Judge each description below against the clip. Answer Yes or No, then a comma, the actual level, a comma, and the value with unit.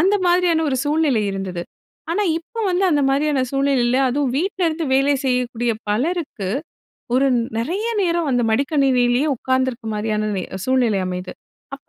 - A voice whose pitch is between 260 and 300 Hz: Yes, very high, 270 Hz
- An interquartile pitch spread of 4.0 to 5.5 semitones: Yes, average, 5.0 semitones